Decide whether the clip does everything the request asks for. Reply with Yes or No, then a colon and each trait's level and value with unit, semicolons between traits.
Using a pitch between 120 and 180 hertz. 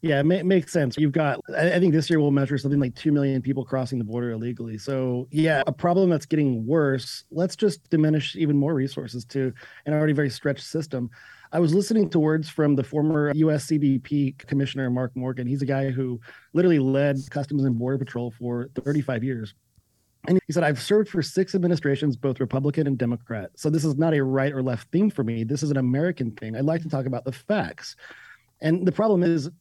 Yes: medium, 140 Hz